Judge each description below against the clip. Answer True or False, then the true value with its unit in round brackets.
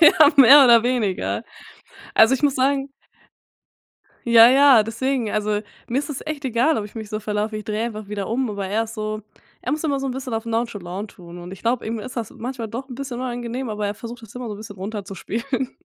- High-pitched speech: True (230 Hz)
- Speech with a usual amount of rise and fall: True (3.6 semitones)